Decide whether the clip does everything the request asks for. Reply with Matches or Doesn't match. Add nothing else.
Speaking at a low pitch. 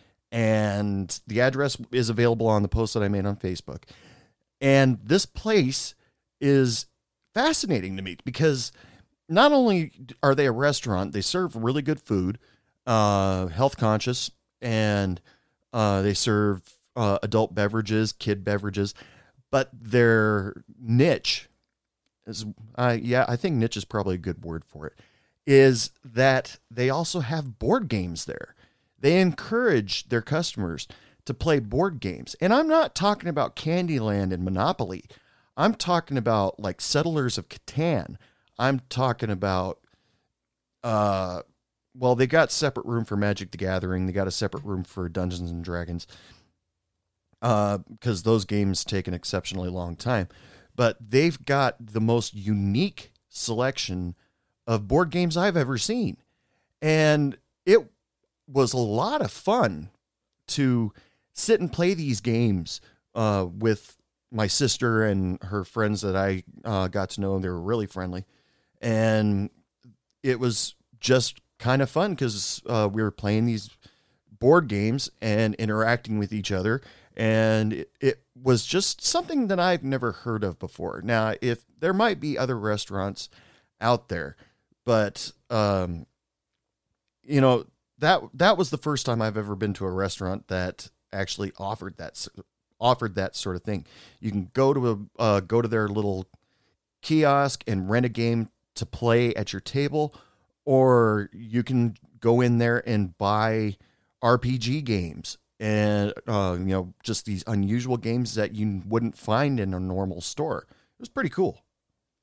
Matches